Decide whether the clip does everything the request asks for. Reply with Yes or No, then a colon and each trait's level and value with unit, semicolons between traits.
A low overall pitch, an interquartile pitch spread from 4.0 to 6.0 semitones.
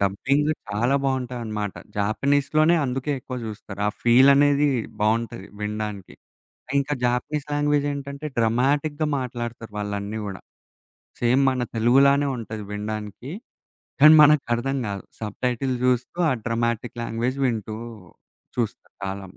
Yes: low, 120 Hz; average, 4.5 semitones